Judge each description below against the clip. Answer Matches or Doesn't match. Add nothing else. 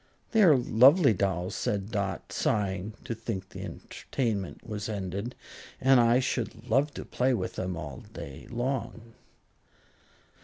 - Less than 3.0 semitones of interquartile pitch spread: Doesn't match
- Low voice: Matches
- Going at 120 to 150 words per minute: Matches